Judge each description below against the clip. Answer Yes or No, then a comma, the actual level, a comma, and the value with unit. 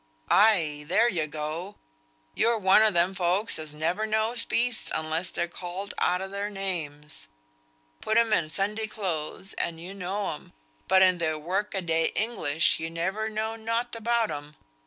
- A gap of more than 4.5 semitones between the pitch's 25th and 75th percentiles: Yes, average, 4.9 semitones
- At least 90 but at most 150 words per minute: No, average, 170 wpm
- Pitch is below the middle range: No, high, 190 Hz